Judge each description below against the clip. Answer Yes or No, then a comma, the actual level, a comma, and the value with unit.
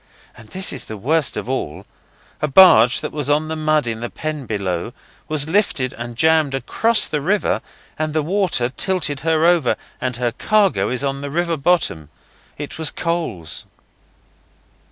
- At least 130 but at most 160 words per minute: No, average, 170 wpm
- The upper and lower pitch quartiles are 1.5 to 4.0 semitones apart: No, average, 4.8 semitones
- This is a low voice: No, medium, 150 Hz